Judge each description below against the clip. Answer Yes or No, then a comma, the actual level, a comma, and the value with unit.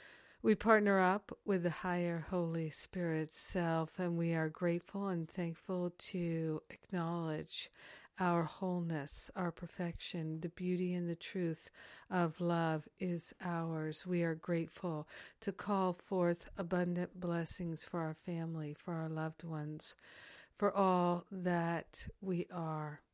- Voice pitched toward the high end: No, medium, 175 Hz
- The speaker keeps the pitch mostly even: Yes, narrow, 1.9 semitones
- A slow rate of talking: Yes, slow, 130 wpm